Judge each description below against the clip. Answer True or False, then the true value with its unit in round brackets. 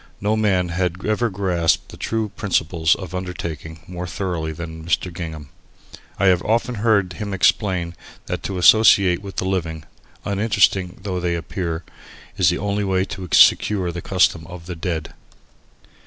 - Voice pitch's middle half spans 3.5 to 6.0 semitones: False (2.8 semitones)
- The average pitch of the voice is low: True (90 Hz)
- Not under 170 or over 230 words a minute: False (155 wpm)